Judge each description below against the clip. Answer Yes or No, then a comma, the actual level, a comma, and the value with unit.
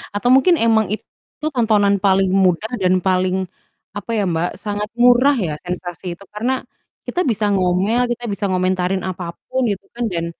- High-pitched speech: Yes, high, 200 Hz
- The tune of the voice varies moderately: Yes, average, 3.9 semitones